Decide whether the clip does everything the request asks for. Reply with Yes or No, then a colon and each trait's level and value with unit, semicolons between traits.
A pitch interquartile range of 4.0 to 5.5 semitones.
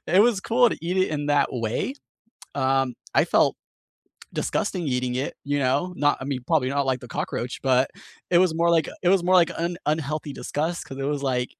Yes: average, 4.6 semitones